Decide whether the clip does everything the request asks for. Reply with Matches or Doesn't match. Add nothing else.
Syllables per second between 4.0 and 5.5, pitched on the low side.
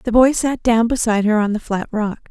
Doesn't match